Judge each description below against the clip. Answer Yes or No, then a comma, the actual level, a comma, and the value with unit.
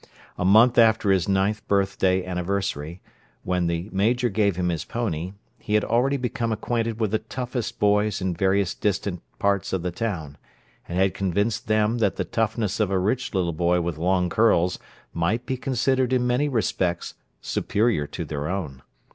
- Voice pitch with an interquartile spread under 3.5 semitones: No, average, 4.0 semitones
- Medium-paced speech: Yes, average, 170 wpm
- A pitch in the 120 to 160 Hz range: No, low, 100 Hz